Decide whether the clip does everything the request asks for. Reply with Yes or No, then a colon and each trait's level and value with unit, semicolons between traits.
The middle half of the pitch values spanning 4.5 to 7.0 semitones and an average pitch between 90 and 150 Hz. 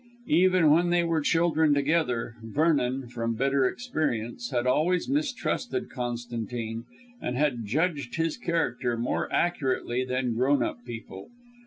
Yes: wide, 5.4 semitones; low, 135 Hz